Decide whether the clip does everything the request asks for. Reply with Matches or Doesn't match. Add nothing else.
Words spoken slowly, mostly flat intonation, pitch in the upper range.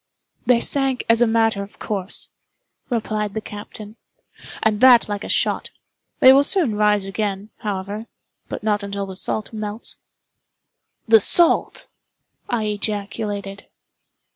Matches